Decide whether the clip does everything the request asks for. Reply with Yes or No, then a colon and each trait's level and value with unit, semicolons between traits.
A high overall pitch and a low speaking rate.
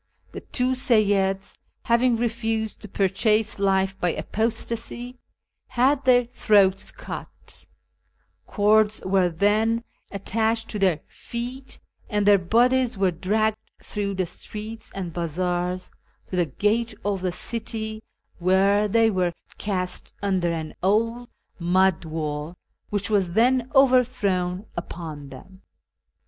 Yes: high, 205 Hz; slow, 120 wpm